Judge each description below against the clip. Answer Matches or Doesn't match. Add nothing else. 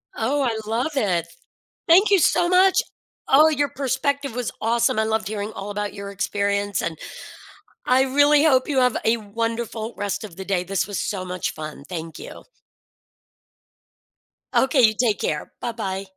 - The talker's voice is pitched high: Matches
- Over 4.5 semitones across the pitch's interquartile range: Matches